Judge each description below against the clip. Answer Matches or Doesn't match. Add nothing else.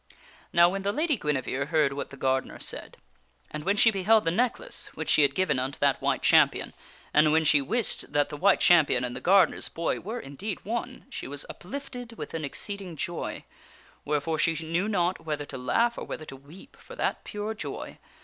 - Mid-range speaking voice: Matches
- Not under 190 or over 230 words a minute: Matches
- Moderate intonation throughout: Doesn't match